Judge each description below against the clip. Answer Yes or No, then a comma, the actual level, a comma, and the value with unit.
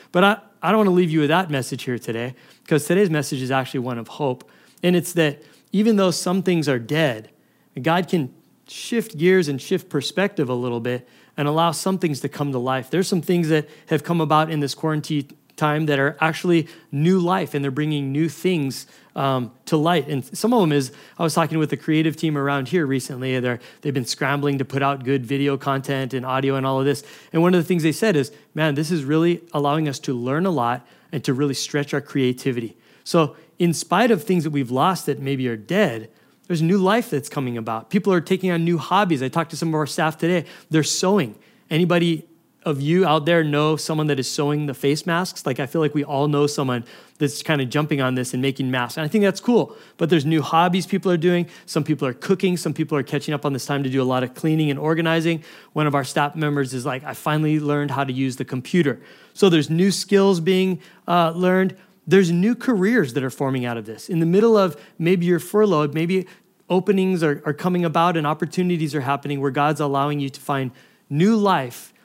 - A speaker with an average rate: No, fast, 230 wpm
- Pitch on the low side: No, medium, 155 Hz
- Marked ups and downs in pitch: No, average, 4.1 semitones